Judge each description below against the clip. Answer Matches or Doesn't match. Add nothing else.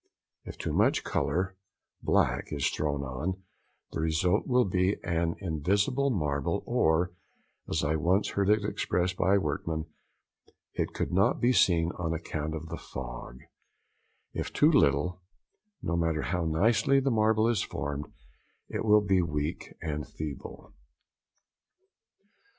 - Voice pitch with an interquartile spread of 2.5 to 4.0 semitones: Doesn't match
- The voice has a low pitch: Matches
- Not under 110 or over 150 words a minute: Matches